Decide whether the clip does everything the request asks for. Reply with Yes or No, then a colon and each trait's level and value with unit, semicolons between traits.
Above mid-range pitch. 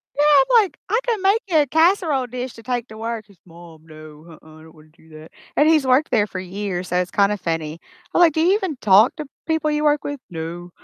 Yes: high, 230 Hz